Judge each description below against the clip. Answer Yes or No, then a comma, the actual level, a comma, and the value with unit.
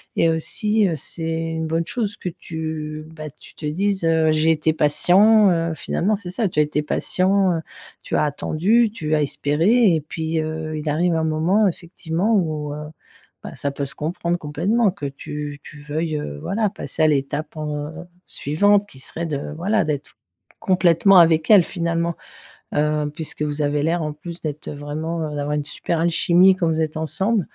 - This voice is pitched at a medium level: Yes, medium, 160 Hz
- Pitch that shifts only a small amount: No, average, 3.0 semitones